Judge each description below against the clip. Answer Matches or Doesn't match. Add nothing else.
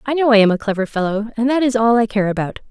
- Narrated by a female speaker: Matches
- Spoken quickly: Matches